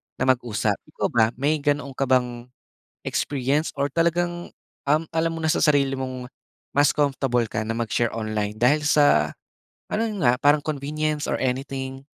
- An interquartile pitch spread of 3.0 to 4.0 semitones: Yes, average, 3.5 semitones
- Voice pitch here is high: No, medium, 140 Hz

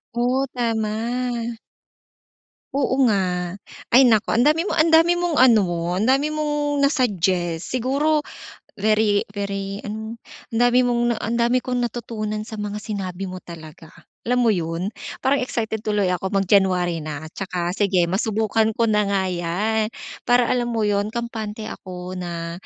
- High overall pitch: Yes, high, 215 Hz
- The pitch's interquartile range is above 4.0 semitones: Yes, average, 4.7 semitones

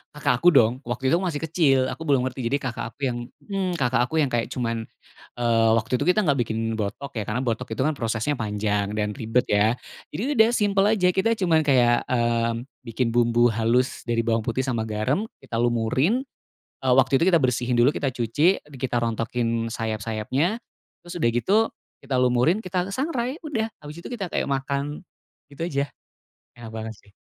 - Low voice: Yes, low, 125 Hz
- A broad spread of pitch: Yes, wide, 5.7 semitones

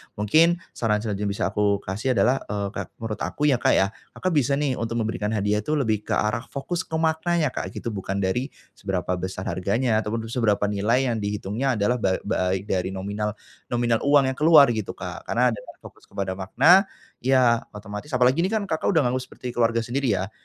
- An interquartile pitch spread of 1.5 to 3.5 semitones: No, average, 4.7 semitones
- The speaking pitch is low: Yes, low, 115 Hz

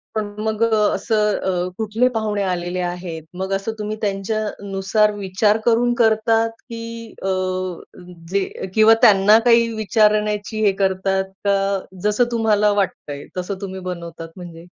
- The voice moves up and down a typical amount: No, narrow, 2.3 semitones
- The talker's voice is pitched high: Yes, high, 205 Hz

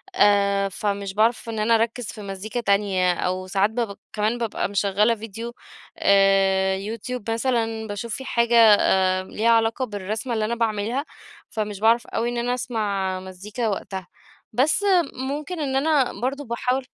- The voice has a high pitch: Yes, high, 220 Hz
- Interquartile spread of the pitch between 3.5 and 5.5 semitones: No, average, 3.1 semitones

